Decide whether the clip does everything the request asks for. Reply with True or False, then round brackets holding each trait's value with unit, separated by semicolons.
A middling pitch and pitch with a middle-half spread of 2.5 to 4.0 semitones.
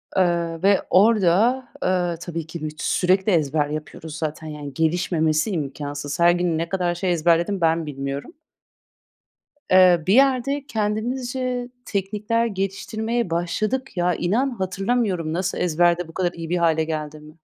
False (175 Hz; 4.4 semitones)